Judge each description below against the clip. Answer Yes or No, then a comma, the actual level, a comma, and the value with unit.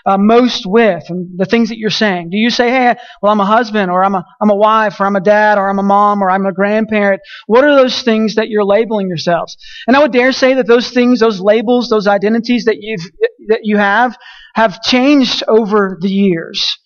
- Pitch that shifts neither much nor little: Yes, average, 3.3 semitones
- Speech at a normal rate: No, fast, 230 wpm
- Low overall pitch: No, high, 220 Hz